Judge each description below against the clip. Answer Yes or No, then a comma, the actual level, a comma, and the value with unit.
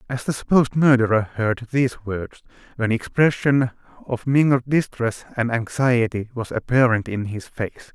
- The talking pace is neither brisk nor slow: Yes, average, 145 wpm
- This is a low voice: Yes, low, 120 Hz